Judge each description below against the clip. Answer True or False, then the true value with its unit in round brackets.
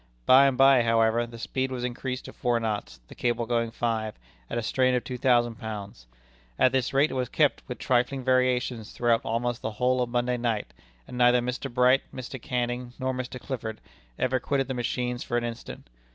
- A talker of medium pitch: False (125 Hz)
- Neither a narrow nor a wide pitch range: False (1.5 semitones)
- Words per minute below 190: False (200 wpm)